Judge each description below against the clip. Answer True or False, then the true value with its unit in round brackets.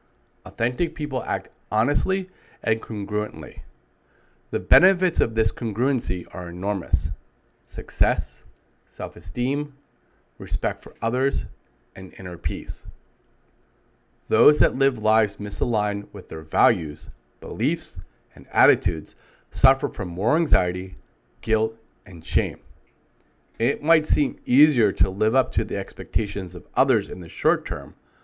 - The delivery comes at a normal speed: False (120 wpm)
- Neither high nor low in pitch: False (105 Hz)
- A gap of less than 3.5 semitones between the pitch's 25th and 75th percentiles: False (5.3 semitones)